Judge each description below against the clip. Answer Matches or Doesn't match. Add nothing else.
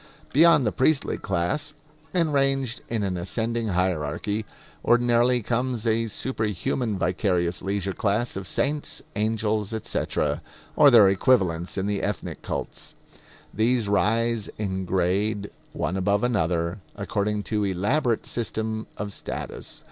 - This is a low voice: Matches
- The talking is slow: Matches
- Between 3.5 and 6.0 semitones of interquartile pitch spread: Matches